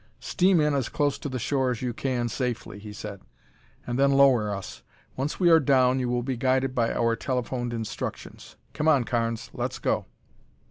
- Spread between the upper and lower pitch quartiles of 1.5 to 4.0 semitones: Yes, average, 2.9 semitones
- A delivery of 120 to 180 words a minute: No, average, 190 wpm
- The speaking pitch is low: Yes, low, 125 Hz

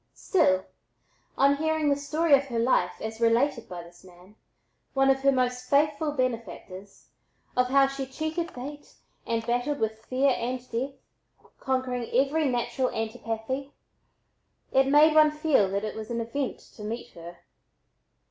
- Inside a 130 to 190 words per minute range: Yes, average, 150 wpm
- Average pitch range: Yes, average, 3.8 semitones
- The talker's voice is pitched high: Yes, very high, 255 Hz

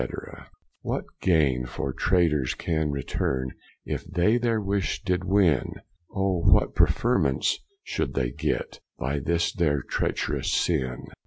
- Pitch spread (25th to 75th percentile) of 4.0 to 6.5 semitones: Yes, wide, 5.6 semitones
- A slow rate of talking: Yes, slow, 120 wpm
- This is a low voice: Yes, very low, 80 Hz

